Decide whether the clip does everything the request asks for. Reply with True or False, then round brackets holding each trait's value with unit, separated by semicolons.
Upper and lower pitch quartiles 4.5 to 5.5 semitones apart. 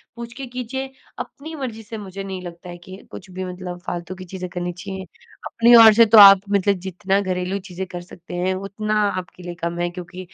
False (2.9 semitones)